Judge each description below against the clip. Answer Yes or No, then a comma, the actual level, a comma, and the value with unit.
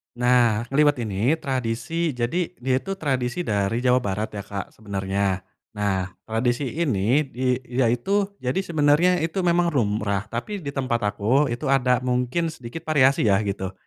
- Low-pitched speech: Yes, low, 125 Hz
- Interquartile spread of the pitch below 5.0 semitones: No, wide, 5.5 semitones